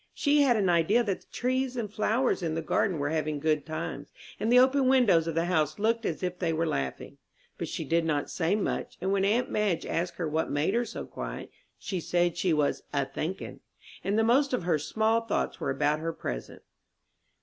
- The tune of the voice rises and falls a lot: Yes, wide, 6.0 semitones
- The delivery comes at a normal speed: No, fast, 220 wpm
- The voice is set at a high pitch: No, medium, 180 Hz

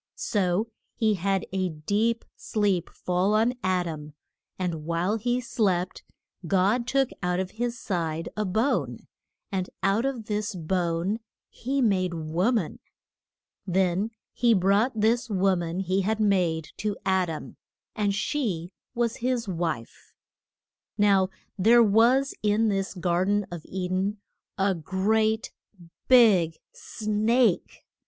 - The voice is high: Yes, high, 195 Hz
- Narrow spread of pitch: No, average, 3.7 semitones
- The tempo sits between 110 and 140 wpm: Yes, slow, 135 wpm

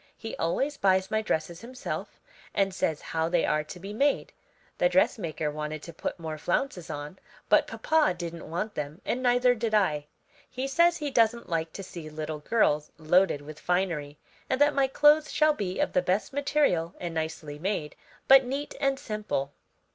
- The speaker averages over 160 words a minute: Yes, average, 180 wpm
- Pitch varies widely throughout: Yes, wide, 8.2 semitones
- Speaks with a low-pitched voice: No, medium, 185 Hz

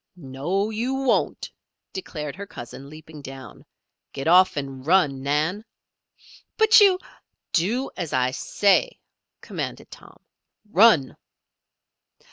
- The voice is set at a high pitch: No, medium, 165 Hz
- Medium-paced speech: No, slow, 110 wpm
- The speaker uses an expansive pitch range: Yes, wide, 7.2 semitones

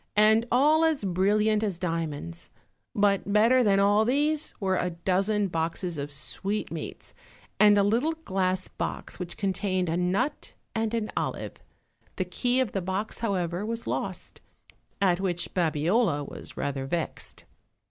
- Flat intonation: No, average, 3.6 semitones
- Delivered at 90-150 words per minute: Yes, average, 145 wpm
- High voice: Yes, high, 195 Hz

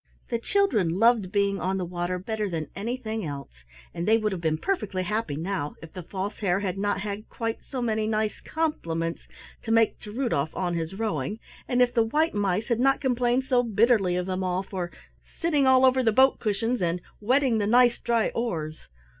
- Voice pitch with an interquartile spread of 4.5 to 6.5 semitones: Yes, average, 4.8 semitones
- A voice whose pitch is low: No, high, 210 Hz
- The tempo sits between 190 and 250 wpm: Yes, average, 200 wpm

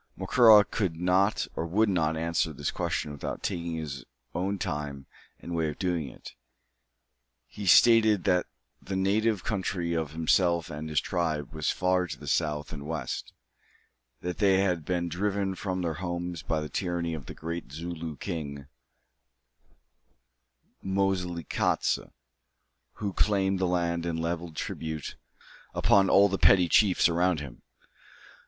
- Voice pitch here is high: No, very low, 85 Hz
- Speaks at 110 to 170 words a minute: Yes, average, 145 wpm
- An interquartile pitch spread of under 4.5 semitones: Yes, average, 3.1 semitones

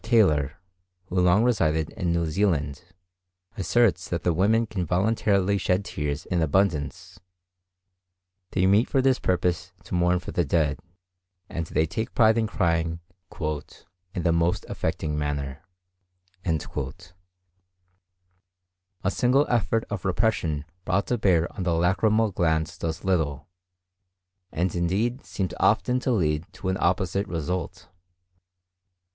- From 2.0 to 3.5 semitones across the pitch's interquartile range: Yes, average, 3.1 semitones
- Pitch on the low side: Yes, very low, 90 Hz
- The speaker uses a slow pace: Yes, slow, 130 wpm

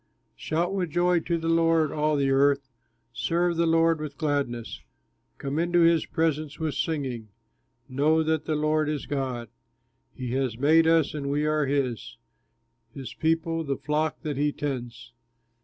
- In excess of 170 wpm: No, average, 155 wpm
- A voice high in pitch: No, medium, 150 Hz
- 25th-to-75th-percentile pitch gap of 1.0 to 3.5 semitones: Yes, average, 2.9 semitones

